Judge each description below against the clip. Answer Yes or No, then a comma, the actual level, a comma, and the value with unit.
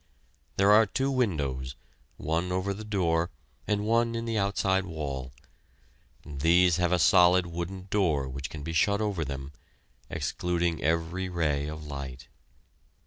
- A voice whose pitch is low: Yes, very low, 85 Hz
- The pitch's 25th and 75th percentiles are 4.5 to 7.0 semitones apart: Yes, average, 4.8 semitones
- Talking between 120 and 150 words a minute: Yes, average, 140 wpm